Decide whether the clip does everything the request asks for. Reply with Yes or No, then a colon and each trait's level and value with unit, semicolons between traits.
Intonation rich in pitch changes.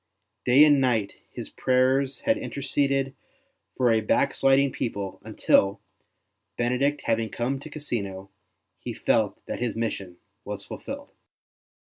No: average, 3.7 semitones